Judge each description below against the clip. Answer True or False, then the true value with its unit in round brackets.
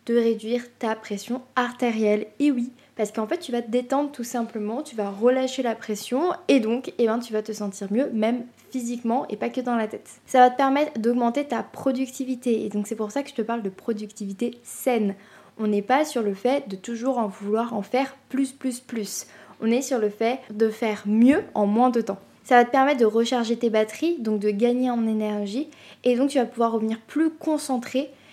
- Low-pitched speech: False (235 Hz)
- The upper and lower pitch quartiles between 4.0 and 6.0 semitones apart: False (3.0 semitones)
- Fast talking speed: True (225 wpm)